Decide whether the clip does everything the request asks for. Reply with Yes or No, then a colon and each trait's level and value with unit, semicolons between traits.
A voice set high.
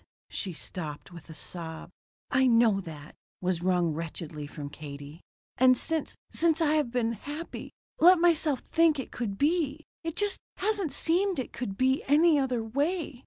Yes: very high, 255 Hz